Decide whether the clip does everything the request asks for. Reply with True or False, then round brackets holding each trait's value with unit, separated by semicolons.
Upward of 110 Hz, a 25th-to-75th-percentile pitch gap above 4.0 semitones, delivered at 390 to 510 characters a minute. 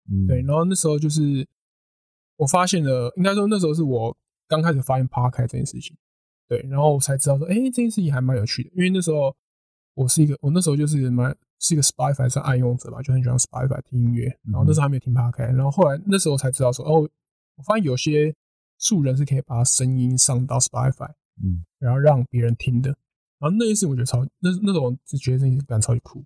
False (135 Hz; 3.6 semitones; 410 characters per minute)